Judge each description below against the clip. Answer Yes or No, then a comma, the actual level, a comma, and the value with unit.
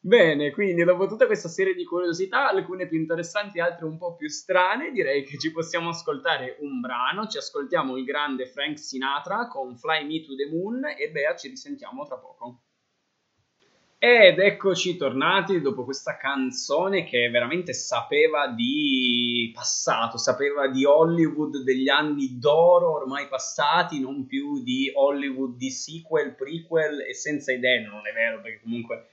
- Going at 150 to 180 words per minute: Yes, average, 155 wpm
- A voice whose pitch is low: No, medium, 160 Hz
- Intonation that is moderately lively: No, wide, 6.6 semitones